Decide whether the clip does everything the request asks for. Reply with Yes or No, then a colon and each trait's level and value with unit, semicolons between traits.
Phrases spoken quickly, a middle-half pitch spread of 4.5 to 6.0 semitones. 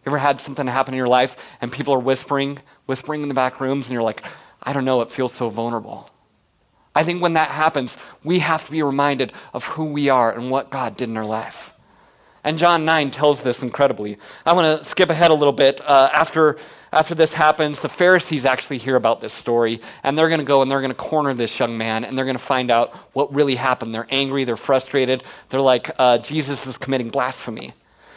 No: fast, 225 wpm; average, 3.1 semitones